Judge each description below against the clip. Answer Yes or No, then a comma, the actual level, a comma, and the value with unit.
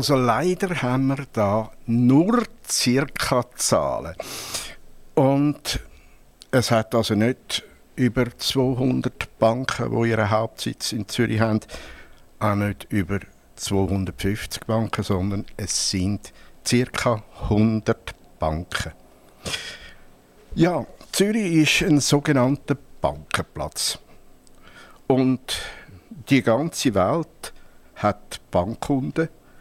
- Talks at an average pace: No, slow, 90 wpm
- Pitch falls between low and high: No, low, 115 Hz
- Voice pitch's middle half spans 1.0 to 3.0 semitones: No, average, 3.9 semitones